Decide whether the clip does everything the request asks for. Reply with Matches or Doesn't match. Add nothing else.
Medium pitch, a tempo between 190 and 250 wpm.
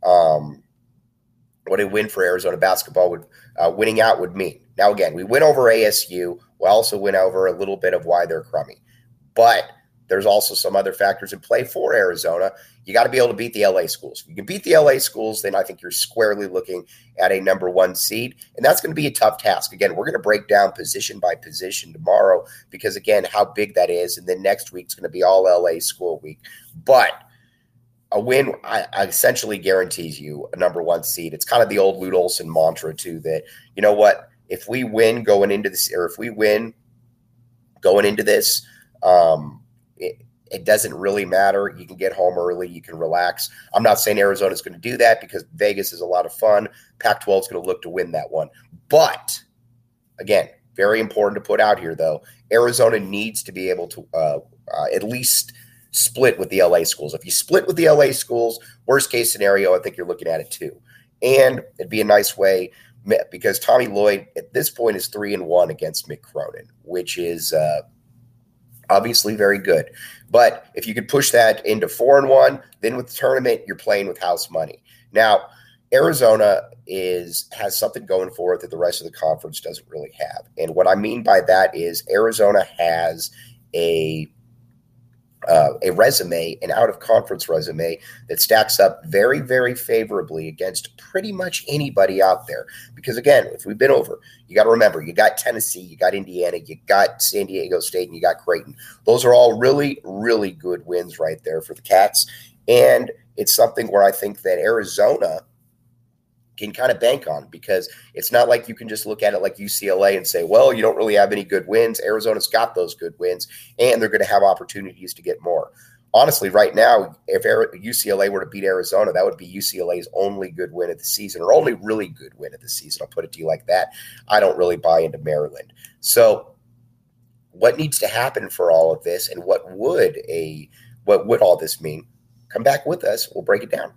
Doesn't match